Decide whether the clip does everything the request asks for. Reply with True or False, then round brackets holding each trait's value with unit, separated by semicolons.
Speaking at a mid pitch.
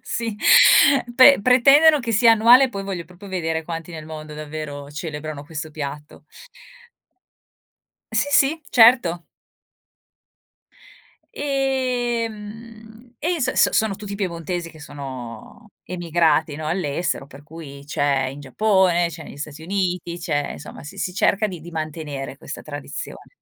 True (175 Hz)